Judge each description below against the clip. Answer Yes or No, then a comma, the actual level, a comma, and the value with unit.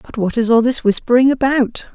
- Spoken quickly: Yes, fast, 215 wpm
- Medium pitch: No, high, 240 Hz